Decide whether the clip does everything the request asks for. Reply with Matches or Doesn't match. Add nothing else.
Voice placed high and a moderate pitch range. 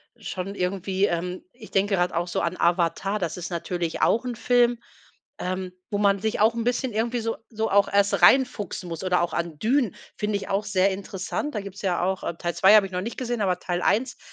Matches